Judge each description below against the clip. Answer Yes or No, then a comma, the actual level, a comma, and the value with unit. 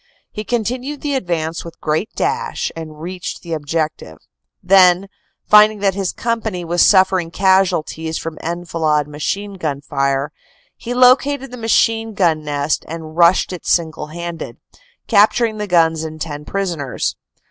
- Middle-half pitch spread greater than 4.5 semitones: Yes, average, 4.9 semitones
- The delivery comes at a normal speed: Yes, average, 145 wpm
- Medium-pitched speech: Yes, medium, 175 Hz